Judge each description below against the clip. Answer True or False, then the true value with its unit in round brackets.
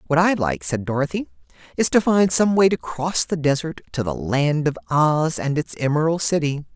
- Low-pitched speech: False (150 Hz)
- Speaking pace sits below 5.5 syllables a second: True (5.0 syllables/s)